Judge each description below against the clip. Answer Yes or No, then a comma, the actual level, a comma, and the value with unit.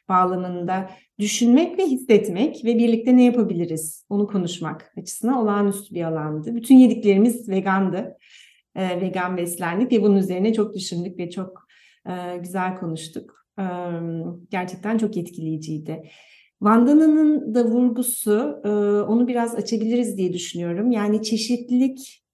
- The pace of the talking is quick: No, average, 120 wpm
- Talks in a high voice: Yes, high, 205 Hz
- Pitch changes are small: No, average, 4.6 semitones